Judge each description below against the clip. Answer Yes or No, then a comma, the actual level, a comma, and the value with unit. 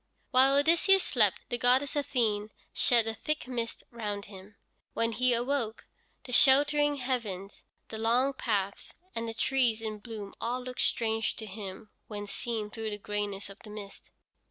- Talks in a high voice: Yes, high, 230 Hz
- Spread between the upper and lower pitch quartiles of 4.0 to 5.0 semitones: No, average, 3.4 semitones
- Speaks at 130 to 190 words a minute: Yes, average, 160 wpm